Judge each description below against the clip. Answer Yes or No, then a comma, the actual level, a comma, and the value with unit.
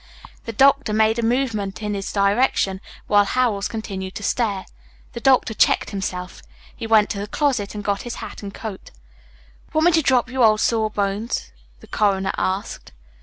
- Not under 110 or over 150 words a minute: No, average, 170 wpm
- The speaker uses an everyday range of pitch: Yes, average, 3.1 semitones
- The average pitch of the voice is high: Yes, high, 215 Hz